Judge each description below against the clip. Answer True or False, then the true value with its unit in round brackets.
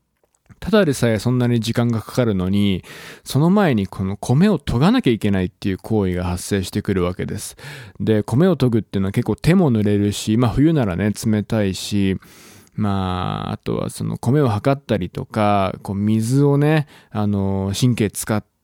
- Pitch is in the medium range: False (110 Hz)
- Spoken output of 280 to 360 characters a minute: True (345 characters per minute)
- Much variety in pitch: False (4.4 semitones)